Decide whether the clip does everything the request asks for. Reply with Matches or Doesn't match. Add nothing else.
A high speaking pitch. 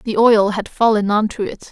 Matches